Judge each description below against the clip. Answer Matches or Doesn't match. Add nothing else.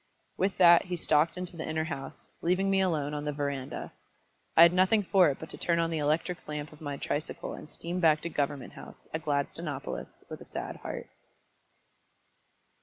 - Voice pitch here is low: Doesn't match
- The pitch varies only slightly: Doesn't match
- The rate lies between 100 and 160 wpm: Doesn't match